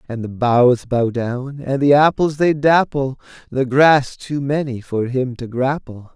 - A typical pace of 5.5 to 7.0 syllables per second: No, 3.9 syllables/s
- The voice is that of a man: Yes, male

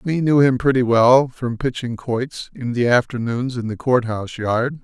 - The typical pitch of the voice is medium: No, low, 125 Hz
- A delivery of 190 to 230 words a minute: Yes, average, 200 wpm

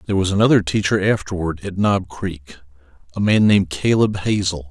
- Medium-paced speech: Yes, average, 155 wpm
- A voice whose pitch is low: Yes, very low, 95 Hz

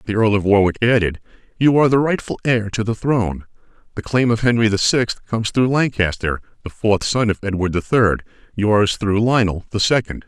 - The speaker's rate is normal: Yes, average, 195 wpm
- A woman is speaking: No, male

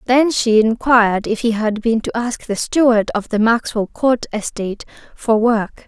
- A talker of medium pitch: No, high, 230 Hz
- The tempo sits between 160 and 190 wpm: Yes, average, 185 wpm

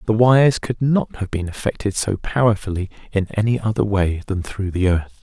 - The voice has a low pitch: Yes, low, 105 Hz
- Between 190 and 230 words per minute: Yes, average, 195 wpm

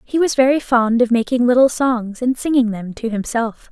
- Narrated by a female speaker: Yes, female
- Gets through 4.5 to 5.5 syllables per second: Yes, 5.0 syllables/s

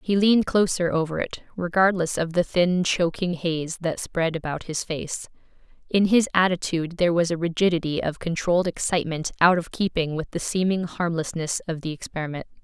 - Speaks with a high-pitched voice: No, medium, 170 Hz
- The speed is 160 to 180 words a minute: Yes, average, 170 wpm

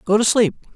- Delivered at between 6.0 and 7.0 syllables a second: Yes, 6.3 syllables/s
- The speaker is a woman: No, male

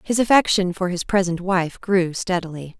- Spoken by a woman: Yes, female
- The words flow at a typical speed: Yes, average, 170 wpm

